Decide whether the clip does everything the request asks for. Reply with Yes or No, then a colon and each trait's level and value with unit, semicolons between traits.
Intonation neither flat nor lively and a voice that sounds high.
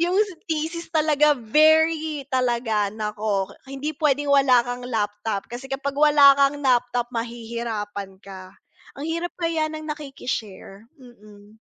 No: wide, 5.7 semitones; very high, 255 Hz